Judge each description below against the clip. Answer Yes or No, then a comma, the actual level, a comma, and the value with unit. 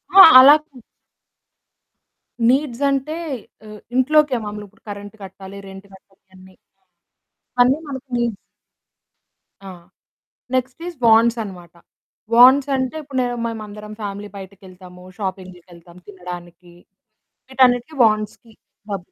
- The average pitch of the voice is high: Yes, high, 215 Hz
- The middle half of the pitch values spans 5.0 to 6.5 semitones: Yes, average, 5.3 semitones